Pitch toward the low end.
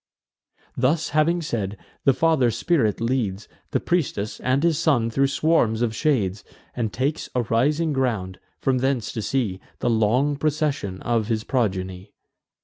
Yes: low, 125 Hz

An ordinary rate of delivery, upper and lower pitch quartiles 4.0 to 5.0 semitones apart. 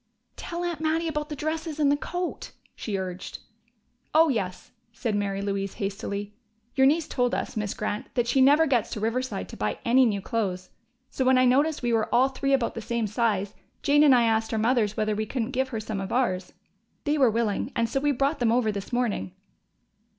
No: fast, 210 wpm; average, 4.7 semitones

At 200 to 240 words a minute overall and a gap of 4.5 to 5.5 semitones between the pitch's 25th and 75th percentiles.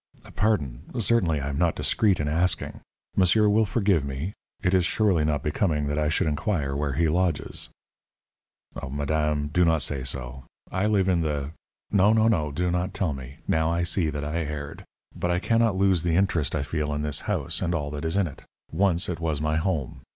No: fast, 205 wpm; average, 4.0 semitones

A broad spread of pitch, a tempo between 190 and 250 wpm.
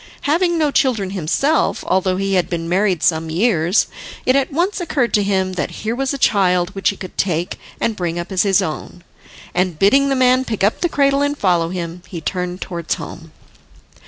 Yes: wide, 6.7 semitones; average, 200 wpm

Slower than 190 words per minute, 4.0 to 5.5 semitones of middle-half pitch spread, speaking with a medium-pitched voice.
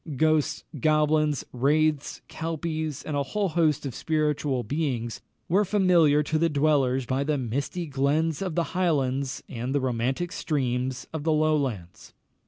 No: average, 145 wpm; average, 3.1 semitones; medium, 150 Hz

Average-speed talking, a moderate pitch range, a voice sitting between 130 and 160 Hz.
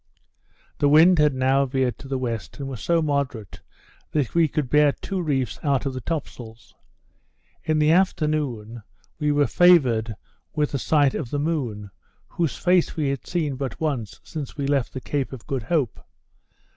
Yes: average, 180 wpm; average, 3.3 semitones; medium, 140 Hz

